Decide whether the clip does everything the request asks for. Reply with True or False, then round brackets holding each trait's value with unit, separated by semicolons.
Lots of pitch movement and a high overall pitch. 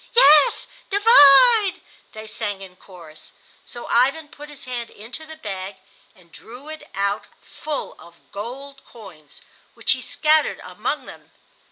True (7.3 semitones; 245 Hz)